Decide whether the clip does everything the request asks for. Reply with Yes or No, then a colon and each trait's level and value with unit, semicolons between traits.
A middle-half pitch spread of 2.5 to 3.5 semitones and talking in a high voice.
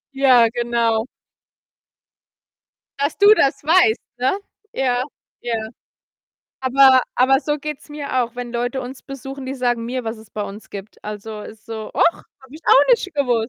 Yes: average, 3.2 semitones; very high, 250 Hz